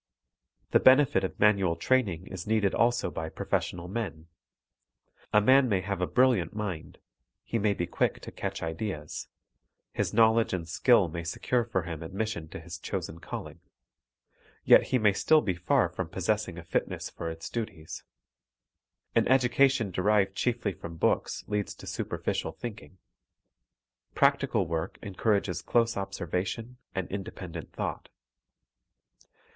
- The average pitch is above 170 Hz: No, low, 100 Hz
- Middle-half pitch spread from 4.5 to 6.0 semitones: Yes, average, 4.8 semitones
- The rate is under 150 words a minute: Yes, average, 140 wpm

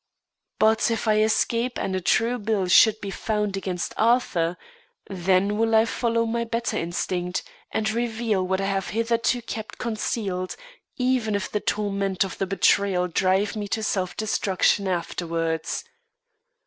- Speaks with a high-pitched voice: Yes, high, 205 Hz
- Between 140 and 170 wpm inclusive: Yes, average, 150 wpm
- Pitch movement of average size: Yes, average, 3.2 semitones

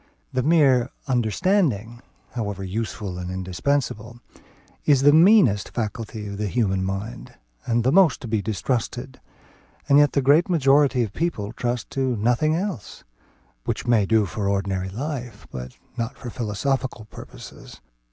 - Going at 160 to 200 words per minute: No, average, 140 wpm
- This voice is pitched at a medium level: No, low, 120 Hz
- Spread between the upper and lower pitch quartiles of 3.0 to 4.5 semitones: No, average, 5.1 semitones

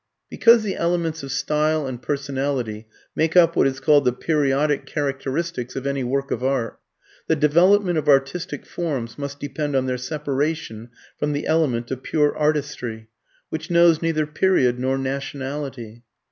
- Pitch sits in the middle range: Yes, medium, 145 Hz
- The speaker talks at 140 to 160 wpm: Yes, average, 155 wpm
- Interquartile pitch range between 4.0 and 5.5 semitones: No, average, 3.1 semitones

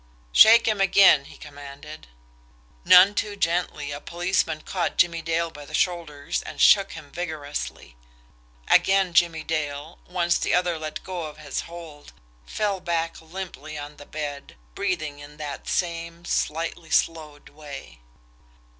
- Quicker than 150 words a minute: No, slow, 135 wpm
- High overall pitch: No, medium, 165 Hz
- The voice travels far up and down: No, average, 3.0 semitones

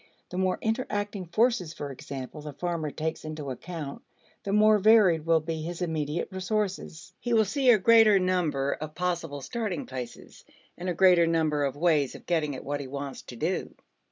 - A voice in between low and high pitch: Yes, medium, 170 Hz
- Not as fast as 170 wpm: No, average, 185 wpm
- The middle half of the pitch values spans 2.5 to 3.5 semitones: No, average, 4.4 semitones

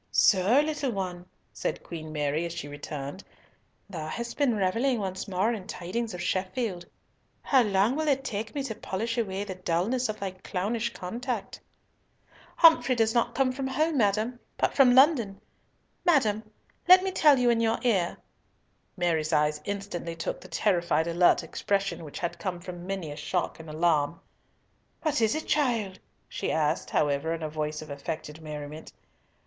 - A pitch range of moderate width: No, wide, 6.0 semitones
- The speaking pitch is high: Yes, high, 195 Hz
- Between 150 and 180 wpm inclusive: Yes, average, 165 wpm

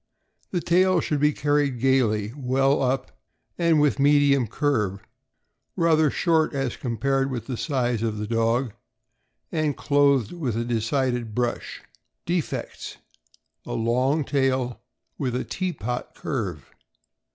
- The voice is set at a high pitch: No, low, 135 Hz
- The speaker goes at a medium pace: No, slow, 130 wpm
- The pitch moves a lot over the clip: No, average, 3.8 semitones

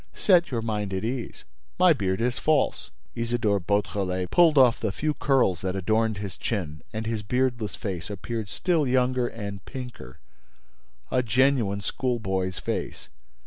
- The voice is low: Yes, low, 110 Hz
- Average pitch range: Yes, average, 4.4 semitones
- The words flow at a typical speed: Yes, average, 145 wpm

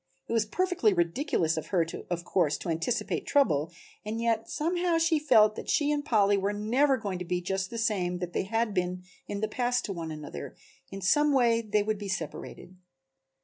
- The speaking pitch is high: Yes, high, 210 Hz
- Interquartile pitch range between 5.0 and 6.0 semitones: Yes, average, 5.3 semitones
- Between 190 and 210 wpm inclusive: Yes, average, 200 wpm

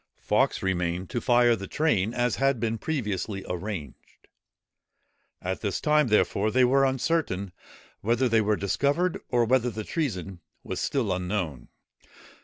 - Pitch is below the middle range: Yes, low, 110 Hz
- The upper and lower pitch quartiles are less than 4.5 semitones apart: No, average, 5.3 semitones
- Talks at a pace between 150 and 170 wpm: No, average, 140 wpm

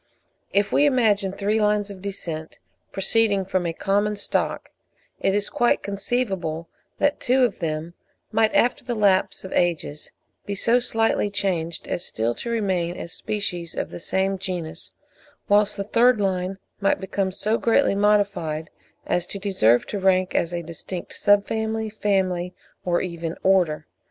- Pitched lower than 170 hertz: No, high, 195 Hz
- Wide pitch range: No, average, 3.2 semitones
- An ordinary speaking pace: Yes, average, 155 wpm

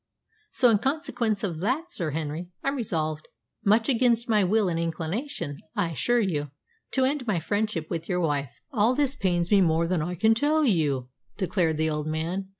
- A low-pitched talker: No, medium, 185 Hz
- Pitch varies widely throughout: Yes, wide, 6.4 semitones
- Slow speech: No, average, 185 wpm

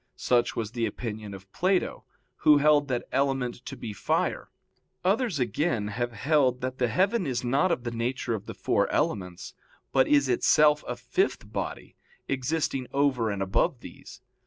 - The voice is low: Yes, low, 125 Hz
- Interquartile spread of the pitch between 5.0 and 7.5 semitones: No, average, 4.0 semitones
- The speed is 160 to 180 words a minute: Yes, average, 165 wpm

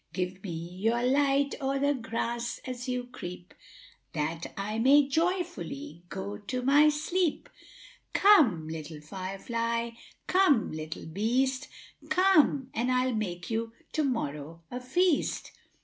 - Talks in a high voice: Yes, high, 240 Hz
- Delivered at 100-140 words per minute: Yes, slow, 135 wpm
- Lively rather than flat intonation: Yes, wide, 6.8 semitones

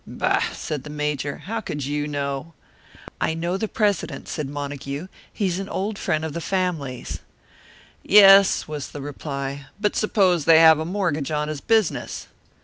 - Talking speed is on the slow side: No, average, 160 wpm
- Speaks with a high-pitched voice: No, medium, 155 Hz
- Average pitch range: Yes, average, 4.7 semitones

